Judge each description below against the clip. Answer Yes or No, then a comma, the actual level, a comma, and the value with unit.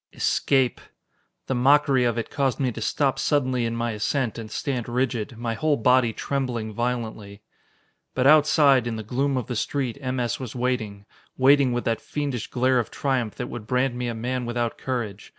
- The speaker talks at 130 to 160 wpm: No, average, 185 wpm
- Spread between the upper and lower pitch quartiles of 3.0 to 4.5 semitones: No, narrow, 2.5 semitones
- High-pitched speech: No, low, 125 Hz